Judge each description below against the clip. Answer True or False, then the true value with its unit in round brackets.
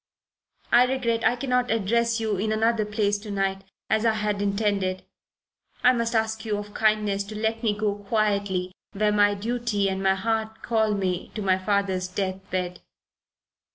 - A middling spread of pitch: False (2.1 semitones)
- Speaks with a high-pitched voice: True (210 Hz)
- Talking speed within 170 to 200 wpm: True (175 wpm)